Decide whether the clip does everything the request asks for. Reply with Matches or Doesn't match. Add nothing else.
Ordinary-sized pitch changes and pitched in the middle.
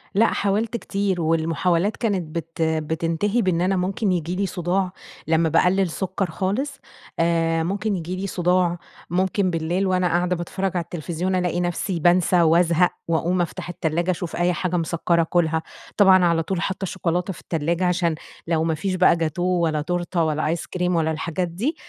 Doesn't match